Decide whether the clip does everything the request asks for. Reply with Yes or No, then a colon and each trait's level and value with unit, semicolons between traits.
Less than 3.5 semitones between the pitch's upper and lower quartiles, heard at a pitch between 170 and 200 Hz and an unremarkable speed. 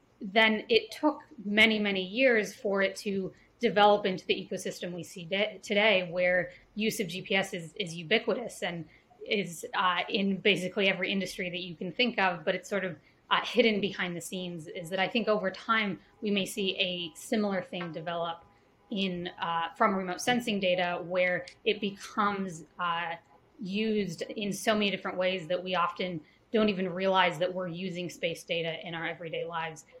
Yes: average, 2.8 semitones; high, 190 Hz; average, 180 wpm